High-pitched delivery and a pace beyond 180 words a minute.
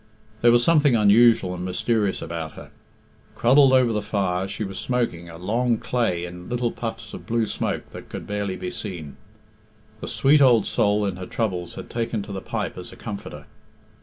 No: low, 105 Hz; average, 190 wpm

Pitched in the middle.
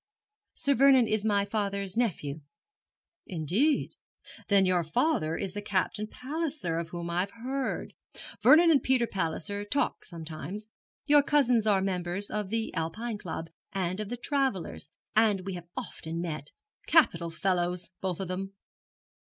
No: high, 195 Hz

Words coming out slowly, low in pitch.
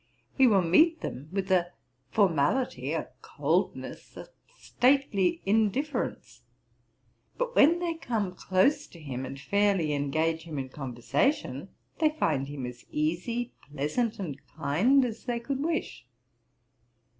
No: slow, 130 wpm; high, 195 Hz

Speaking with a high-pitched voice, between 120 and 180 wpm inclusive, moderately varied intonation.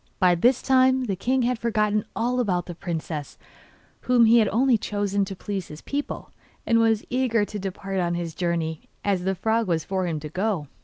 No: high, 205 Hz; fast, 205 wpm; average, 4.7 semitones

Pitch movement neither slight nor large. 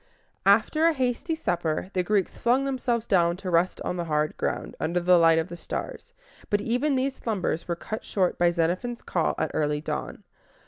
No: wide, 6.0 semitones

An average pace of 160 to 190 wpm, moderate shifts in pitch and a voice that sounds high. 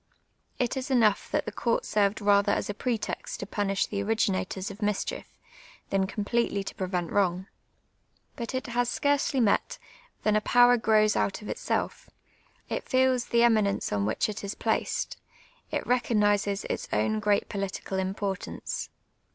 Yes: average, 165 wpm; average, 3.0 semitones; high, 210 Hz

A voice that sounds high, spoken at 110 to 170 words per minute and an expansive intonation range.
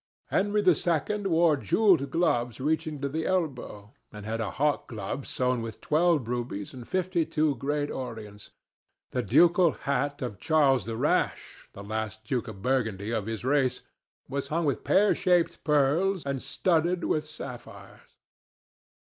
No: medium, 140 Hz; average, 150 wpm; wide, 6.1 semitones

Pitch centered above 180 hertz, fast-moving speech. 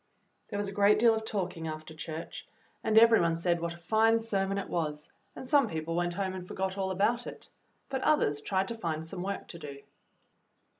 Yes: high, 190 Hz; fast, 210 wpm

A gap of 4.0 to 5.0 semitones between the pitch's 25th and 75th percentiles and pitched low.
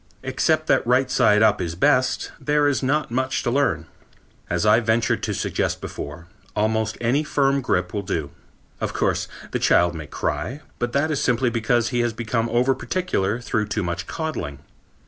Yes: average, 4.3 semitones; low, 120 Hz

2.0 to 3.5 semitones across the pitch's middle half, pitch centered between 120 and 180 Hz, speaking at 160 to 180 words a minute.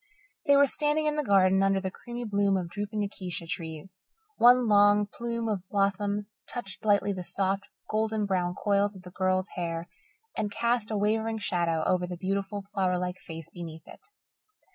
No: average, 2.7 semitones; high, 200 Hz; average, 175 wpm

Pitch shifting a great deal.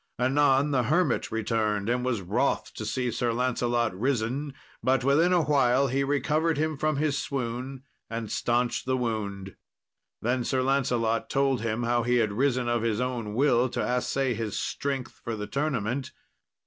No: average, 3.0 semitones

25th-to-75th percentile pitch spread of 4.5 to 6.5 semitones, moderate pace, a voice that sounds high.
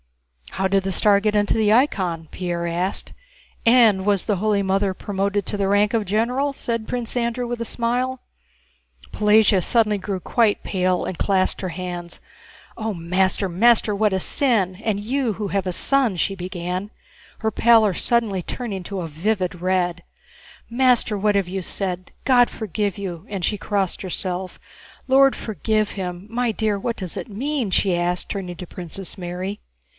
No: average, 3.3 semitones; average, 170 wpm; high, 200 Hz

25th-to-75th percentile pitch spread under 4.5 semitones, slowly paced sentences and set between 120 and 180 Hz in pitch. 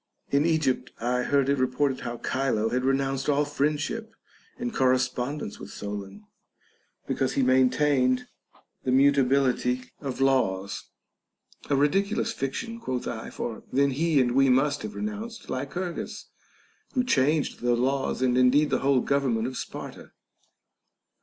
No: narrow, 2.5 semitones; average, 145 wpm; low, 135 Hz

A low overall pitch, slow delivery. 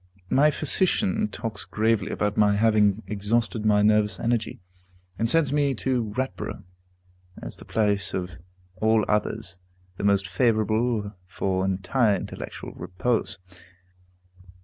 Yes: low, 110 Hz; slow, 120 wpm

